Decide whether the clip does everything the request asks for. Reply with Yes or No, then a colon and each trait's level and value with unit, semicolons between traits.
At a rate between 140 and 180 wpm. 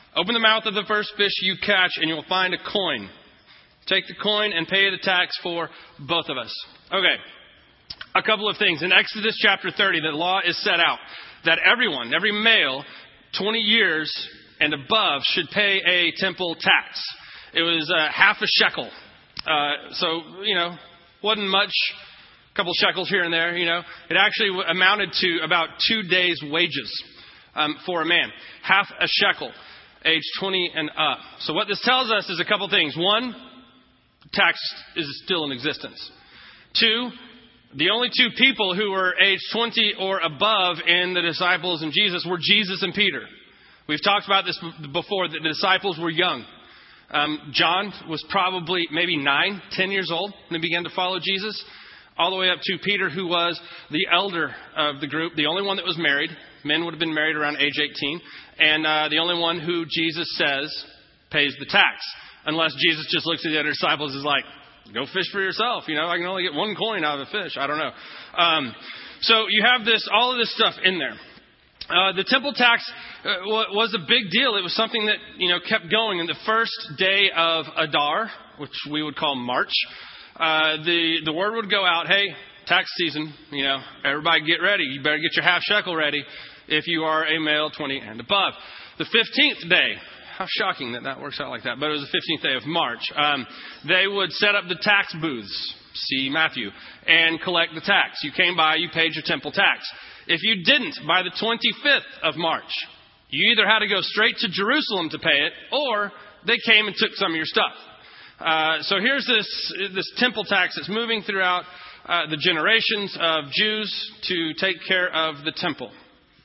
No: average, 195 wpm